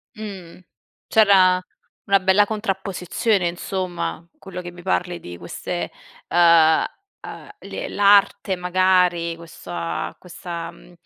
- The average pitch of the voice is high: No, medium, 180 Hz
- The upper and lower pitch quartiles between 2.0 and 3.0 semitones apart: Yes, narrow, 2.3 semitones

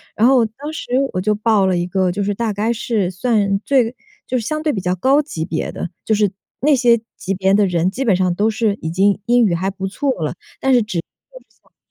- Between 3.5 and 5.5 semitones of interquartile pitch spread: Yes, average, 4.2 semitones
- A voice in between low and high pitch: No, high, 210 Hz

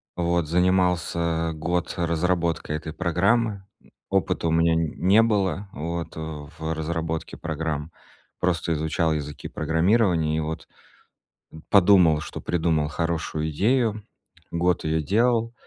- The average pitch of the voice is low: Yes, very low, 85 Hz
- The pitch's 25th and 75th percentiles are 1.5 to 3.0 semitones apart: Yes, narrow, 2.6 semitones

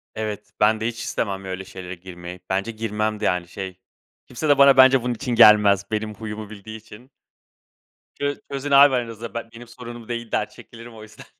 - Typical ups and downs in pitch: Yes, average, 3.1 semitones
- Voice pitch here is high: No, low, 110 Hz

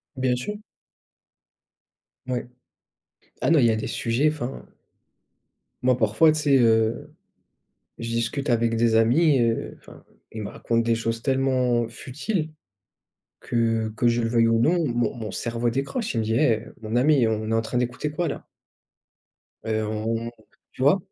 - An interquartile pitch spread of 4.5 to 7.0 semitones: No, average, 2.8 semitones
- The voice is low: Yes, low, 120 Hz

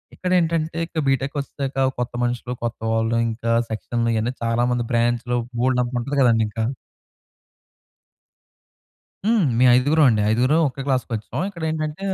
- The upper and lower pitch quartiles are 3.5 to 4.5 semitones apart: Yes, average, 3.8 semitones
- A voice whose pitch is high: No, low, 125 Hz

